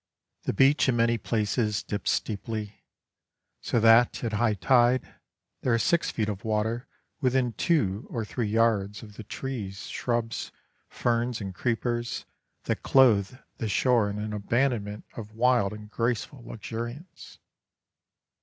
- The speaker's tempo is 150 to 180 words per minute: No, slow, 135 wpm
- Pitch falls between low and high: No, low, 115 Hz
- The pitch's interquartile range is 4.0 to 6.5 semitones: No, narrow, 2.5 semitones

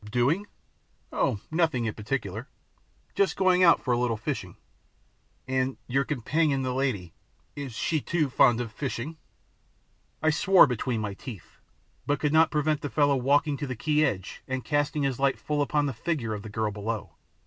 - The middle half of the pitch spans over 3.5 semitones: Yes, average, 4.5 semitones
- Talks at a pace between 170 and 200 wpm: Yes, average, 175 wpm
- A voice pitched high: No, low, 135 Hz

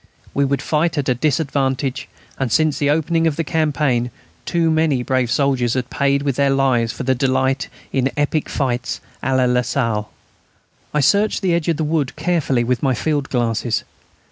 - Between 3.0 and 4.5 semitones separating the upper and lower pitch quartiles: Yes, average, 3.3 semitones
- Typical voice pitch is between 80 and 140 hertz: Yes, low, 135 Hz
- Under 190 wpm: Yes, average, 180 wpm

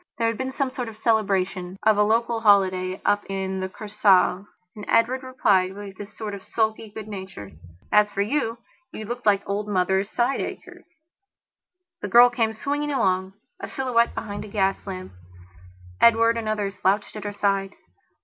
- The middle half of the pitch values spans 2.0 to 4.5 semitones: Yes, average, 2.9 semitones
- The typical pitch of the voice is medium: No, high, 210 Hz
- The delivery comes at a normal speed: Yes, average, 170 wpm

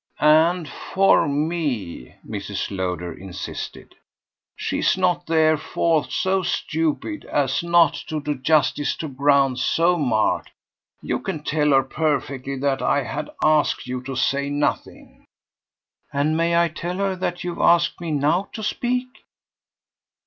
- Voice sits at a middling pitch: Yes, medium, 150 Hz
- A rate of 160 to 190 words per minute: No, slow, 135 wpm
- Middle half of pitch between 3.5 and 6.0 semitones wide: Yes, average, 3.8 semitones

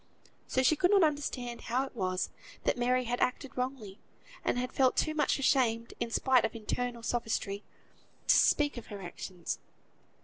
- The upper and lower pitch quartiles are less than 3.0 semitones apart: Yes, narrow, 2.6 semitones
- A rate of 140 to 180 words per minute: Yes, average, 175 wpm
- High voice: Yes, high, 245 Hz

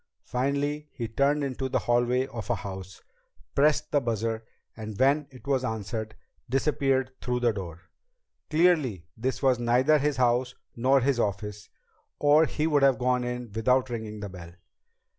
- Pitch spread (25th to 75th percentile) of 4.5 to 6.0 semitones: No, average, 3.7 semitones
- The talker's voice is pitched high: No, low, 125 Hz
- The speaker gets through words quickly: No, average, 160 wpm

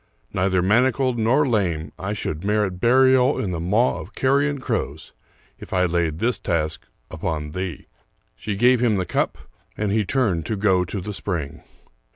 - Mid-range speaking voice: No, low, 100 Hz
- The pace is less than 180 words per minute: Yes, average, 170 wpm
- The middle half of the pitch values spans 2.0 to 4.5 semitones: No, wide, 5.5 semitones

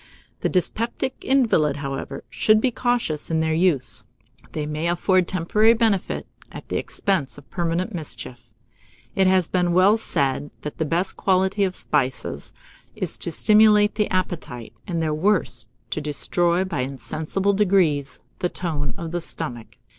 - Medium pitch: Yes, medium, 175 Hz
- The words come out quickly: No, average, 150 wpm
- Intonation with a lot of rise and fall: No, average, 4.6 semitones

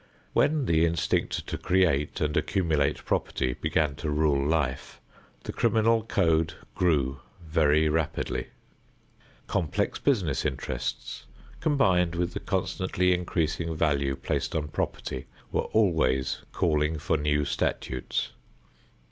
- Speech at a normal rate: No, slow, 115 wpm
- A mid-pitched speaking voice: No, very low, 80 Hz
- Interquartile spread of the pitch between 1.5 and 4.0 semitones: Yes, average, 3.3 semitones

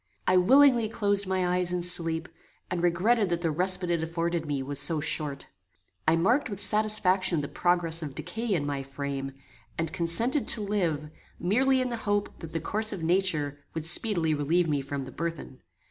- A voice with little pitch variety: No, average, 4.3 semitones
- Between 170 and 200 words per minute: Yes, average, 185 wpm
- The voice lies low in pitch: No, medium, 175 Hz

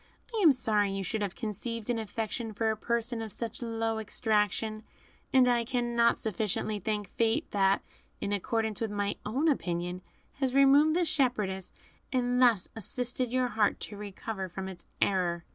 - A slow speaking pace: No, average, 165 wpm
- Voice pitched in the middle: No, high, 220 Hz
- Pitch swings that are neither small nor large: Yes, average, 3.1 semitones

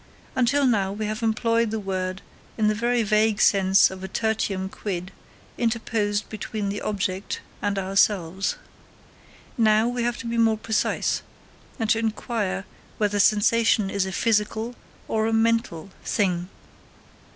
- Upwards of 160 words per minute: No, average, 140 wpm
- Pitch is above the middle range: Yes, high, 215 Hz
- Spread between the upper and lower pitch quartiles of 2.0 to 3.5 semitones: Yes, narrow, 2.6 semitones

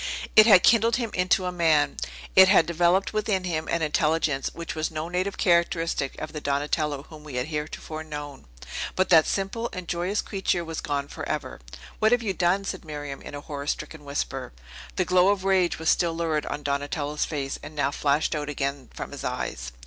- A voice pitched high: No, medium, 160 Hz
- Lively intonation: No, average, 3.9 semitones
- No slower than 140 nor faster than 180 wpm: No, average, 195 wpm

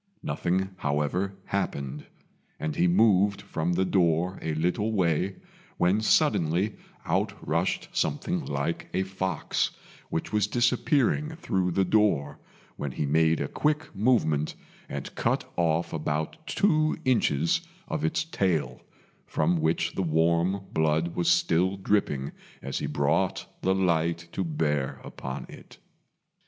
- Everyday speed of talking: No, slow, 130 wpm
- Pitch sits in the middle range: No, very low, 90 Hz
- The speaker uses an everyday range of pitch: Yes, average, 3.9 semitones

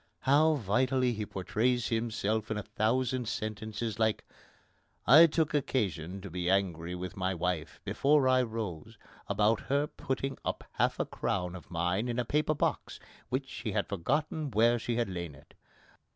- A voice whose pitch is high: No, low, 110 Hz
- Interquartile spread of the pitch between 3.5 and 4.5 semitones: No, average, 5.3 semitones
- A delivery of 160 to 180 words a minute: Yes, average, 165 wpm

